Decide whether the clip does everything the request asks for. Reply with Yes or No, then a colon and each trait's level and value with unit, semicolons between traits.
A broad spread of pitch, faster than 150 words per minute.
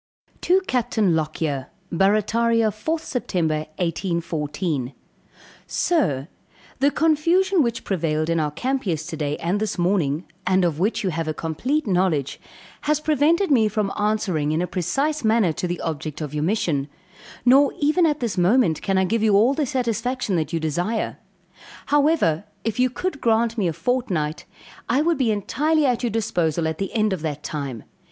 Yes: wide, 7.8 semitones; average, 165 wpm